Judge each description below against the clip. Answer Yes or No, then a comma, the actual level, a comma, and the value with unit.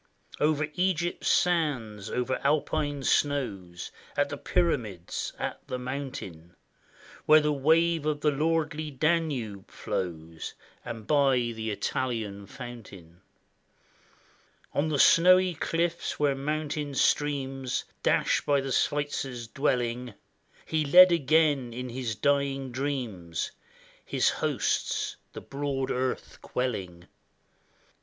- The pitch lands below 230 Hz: Yes, low, 135 Hz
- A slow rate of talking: Yes, slow, 105 wpm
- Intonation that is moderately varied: Yes, average, 4.6 semitones